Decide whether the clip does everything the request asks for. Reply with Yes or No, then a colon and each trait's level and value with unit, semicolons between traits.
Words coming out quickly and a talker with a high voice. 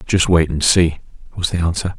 No: fast, 210 wpm; very low, 85 Hz